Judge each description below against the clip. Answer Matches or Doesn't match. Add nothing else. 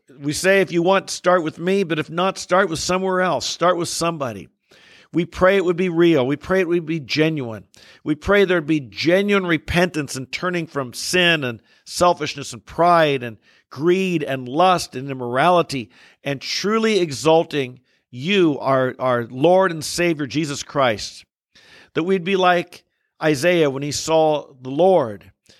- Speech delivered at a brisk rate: Doesn't match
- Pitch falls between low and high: Matches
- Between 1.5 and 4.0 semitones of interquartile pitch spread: Doesn't match